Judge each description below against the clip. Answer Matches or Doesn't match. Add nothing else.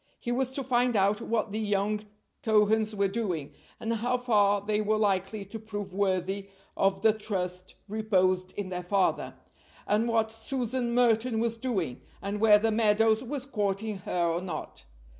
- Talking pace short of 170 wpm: Matches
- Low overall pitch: Doesn't match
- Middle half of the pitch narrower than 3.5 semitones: Matches